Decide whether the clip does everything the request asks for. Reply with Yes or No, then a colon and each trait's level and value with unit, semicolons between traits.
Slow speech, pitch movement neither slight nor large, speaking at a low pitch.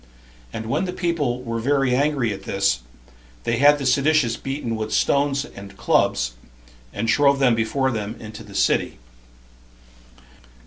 No: average, 145 wpm; average, 4.2 semitones; low, 125 Hz